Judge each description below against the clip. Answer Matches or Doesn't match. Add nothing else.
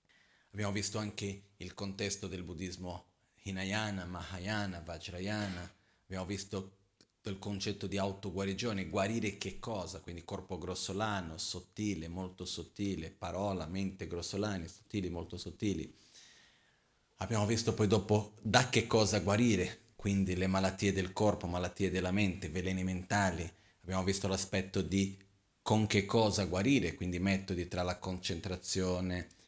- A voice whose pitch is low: Matches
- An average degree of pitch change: Doesn't match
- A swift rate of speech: Doesn't match